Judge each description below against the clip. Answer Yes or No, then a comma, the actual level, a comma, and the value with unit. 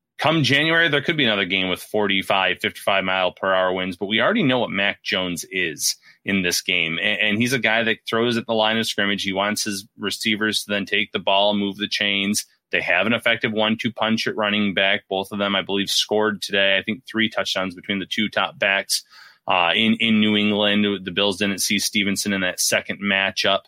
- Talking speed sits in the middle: No, fast, 225 wpm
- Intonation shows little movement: Yes, narrow, 2.0 semitones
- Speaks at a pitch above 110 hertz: No, low, 100 Hz